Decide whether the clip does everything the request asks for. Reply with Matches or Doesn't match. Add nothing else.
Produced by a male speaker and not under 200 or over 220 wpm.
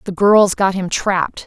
Doesn't match